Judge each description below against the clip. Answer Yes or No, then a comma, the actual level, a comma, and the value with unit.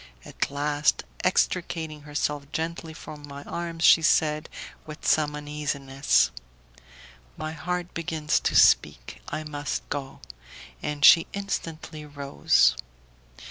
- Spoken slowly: Yes, slow, 110 wpm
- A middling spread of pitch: No, narrow, 1.9 semitones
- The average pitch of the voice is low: No, medium, 150 Hz